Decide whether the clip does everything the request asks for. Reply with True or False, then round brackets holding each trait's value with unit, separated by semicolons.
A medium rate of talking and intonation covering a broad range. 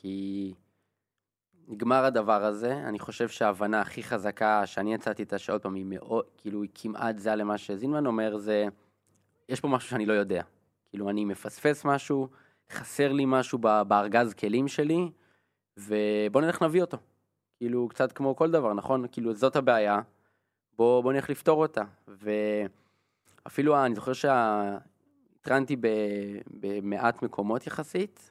False (135 wpm; 4.3 semitones)